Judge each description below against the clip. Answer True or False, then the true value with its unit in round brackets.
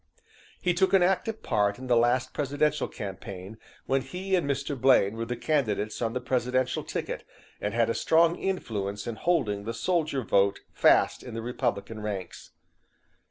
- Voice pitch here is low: True (125 Hz)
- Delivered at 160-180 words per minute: True (165 wpm)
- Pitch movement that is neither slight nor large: False (6.0 semitones)